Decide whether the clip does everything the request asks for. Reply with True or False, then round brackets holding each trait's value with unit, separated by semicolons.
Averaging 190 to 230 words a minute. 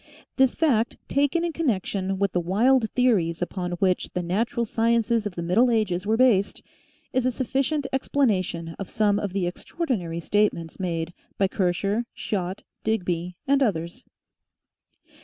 False (155 wpm)